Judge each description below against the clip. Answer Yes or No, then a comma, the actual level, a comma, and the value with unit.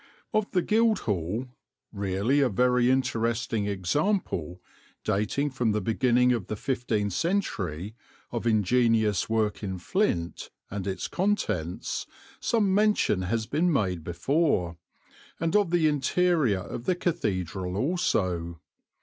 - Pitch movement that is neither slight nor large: No, wide, 8.3 semitones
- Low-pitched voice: Yes, low, 115 Hz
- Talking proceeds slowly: Yes, slow, 120 wpm